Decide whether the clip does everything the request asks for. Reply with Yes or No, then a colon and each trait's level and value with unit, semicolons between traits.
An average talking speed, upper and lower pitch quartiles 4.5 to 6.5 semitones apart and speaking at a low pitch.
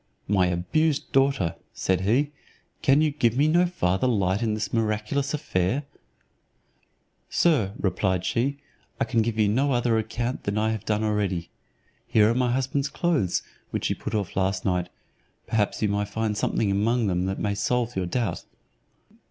Yes: average, 170 wpm; average, 4.8 semitones; low, 110 Hz